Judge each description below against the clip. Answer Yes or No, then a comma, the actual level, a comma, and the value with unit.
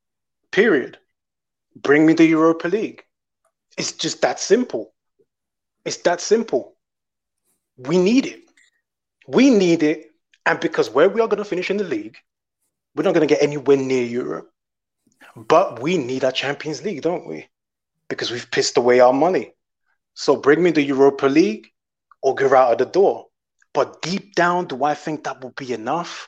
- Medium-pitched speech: Yes, medium, 160 Hz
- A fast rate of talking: No, average, 170 wpm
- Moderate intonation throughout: No, wide, 6.3 semitones